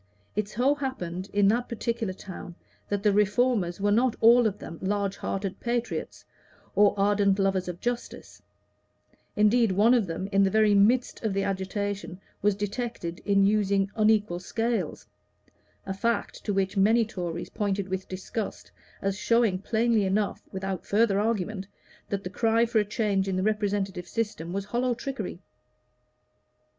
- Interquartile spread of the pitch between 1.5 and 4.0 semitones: Yes, average, 2.8 semitones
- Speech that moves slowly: No, average, 155 wpm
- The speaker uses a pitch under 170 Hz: No, high, 205 Hz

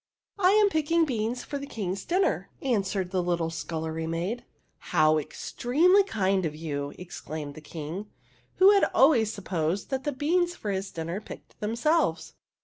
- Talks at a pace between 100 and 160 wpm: No, average, 170 wpm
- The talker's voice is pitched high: Yes, high, 205 Hz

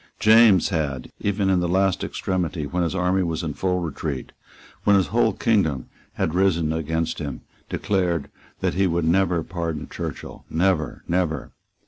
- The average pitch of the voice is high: No, very low, 85 Hz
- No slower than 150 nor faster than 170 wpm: Yes, average, 155 wpm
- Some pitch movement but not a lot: Yes, average, 3.0 semitones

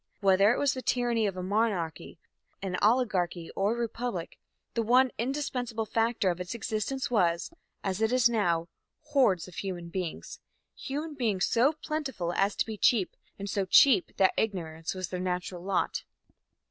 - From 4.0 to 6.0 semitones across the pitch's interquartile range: Yes, average, 5.0 semitones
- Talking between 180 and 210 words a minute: No, average, 165 wpm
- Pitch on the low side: No, high, 210 Hz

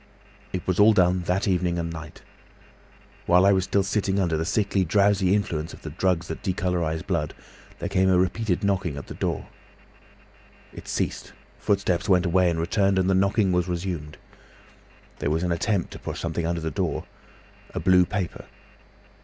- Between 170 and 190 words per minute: Yes, average, 175 wpm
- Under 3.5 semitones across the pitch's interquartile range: Yes, narrow, 2.4 semitones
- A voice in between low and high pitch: No, very low, 90 Hz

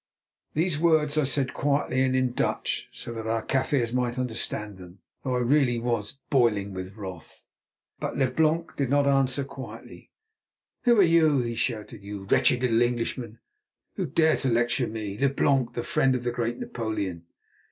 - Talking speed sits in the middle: Yes, average, 170 wpm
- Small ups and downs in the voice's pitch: No, average, 3.6 semitones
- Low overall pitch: Yes, low, 125 Hz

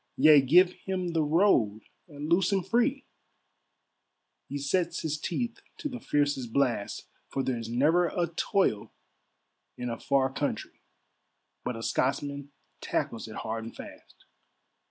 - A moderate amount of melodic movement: No, wide, 5.7 semitones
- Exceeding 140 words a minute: No, slow, 135 wpm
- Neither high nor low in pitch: Yes, medium, 145 Hz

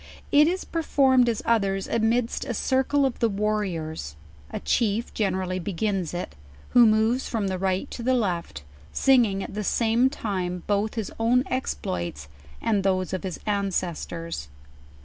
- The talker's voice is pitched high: Yes, high, 210 Hz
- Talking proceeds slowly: No, average, 150 wpm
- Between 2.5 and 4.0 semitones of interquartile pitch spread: No, average, 4.4 semitones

